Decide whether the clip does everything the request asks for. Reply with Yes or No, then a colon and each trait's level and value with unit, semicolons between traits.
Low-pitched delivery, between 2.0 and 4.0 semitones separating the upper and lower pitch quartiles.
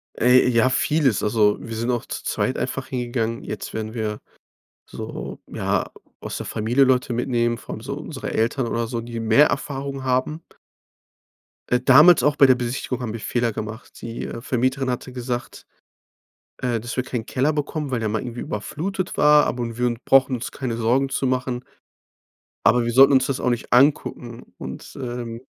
Yes: low, 125 Hz; narrow, 2.4 semitones